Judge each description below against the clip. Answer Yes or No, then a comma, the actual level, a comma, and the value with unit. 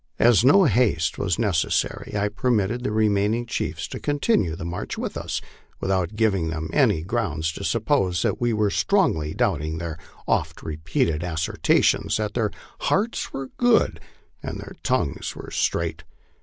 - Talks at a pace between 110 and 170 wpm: Yes, average, 150 wpm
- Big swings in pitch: Yes, wide, 6.5 semitones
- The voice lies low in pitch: Yes, low, 100 Hz